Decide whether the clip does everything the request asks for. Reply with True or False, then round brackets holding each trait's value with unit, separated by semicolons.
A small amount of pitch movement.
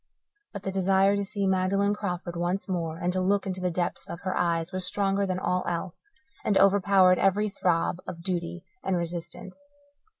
True (1.9 semitones)